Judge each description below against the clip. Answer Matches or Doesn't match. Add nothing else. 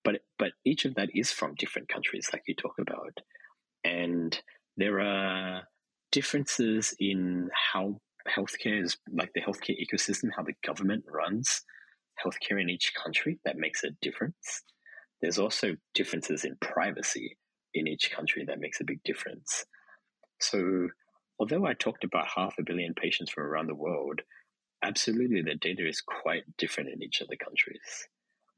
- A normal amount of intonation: Doesn't match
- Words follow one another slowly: Doesn't match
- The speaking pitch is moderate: Doesn't match